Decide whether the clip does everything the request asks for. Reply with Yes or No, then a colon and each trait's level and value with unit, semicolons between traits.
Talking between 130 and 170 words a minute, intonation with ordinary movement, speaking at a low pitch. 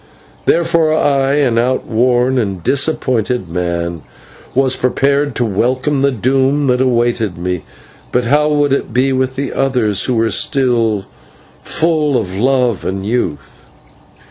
Yes: slow, 135 wpm; average, 3.7 semitones; low, 125 Hz